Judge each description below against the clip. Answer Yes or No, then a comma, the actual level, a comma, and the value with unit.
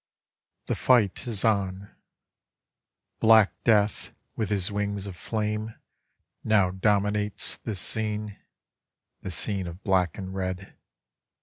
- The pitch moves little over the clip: Yes, narrow, 2.1 semitones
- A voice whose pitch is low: Yes, low, 100 Hz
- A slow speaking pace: Yes, slow, 110 wpm